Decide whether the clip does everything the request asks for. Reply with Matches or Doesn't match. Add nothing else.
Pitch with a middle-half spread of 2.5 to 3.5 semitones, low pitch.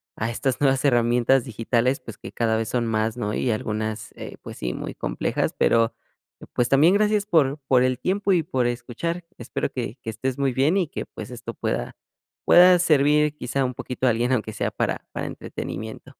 Doesn't match